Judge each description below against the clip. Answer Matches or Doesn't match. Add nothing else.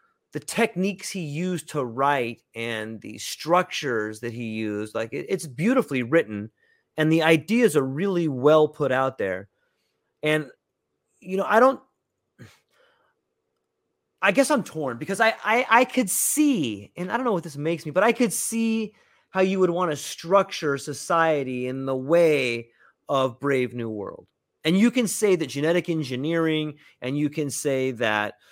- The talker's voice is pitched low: Doesn't match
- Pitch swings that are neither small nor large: Doesn't match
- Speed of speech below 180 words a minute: Matches